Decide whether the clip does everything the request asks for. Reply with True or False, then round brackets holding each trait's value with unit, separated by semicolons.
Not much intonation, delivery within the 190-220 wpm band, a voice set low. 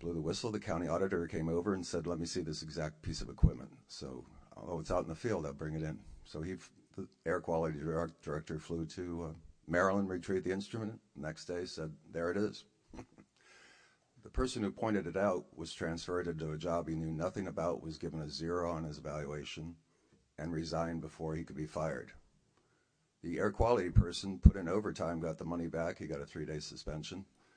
True (2.3 semitones; 205 wpm; 85 Hz)